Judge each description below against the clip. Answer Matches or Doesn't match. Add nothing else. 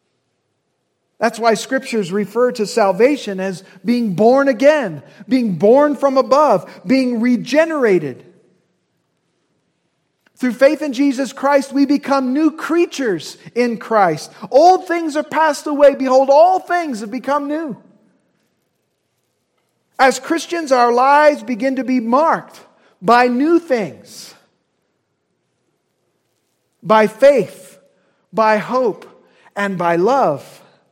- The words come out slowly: Matches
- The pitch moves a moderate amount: Matches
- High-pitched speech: Matches